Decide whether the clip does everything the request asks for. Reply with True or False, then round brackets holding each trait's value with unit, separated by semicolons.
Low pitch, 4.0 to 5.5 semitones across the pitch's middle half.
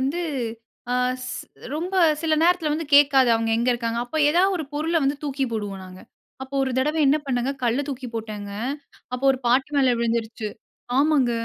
False (265 Hz; 4.3 semitones)